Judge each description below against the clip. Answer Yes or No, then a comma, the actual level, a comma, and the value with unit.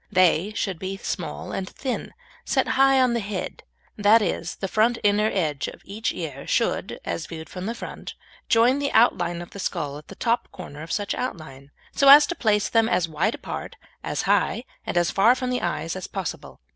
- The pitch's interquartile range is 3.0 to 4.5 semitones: No, average, 5.2 semitones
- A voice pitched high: Yes, high, 195 Hz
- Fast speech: Yes, fast, 210 wpm